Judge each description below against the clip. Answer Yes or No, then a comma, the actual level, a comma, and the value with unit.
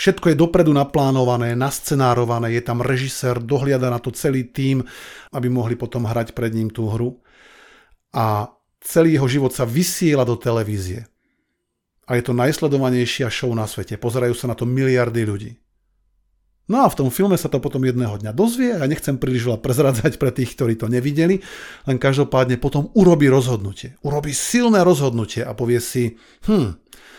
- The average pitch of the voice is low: Yes, low, 125 Hz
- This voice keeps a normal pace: No, fast, 170 wpm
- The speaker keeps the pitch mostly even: No, average, 3.2 semitones